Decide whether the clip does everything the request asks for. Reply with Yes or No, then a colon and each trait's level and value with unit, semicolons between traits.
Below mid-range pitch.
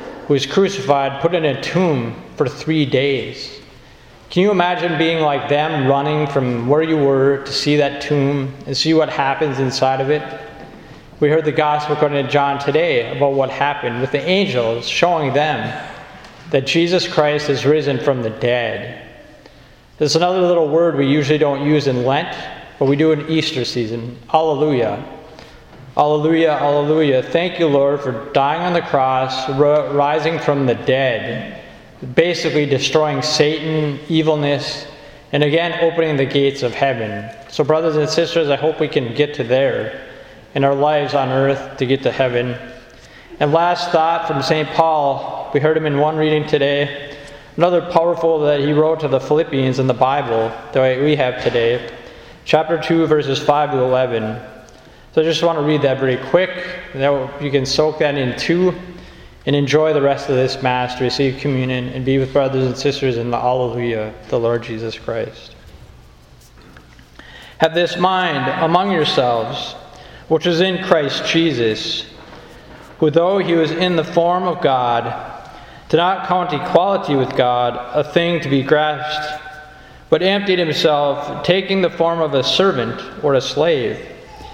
No: medium, 145 Hz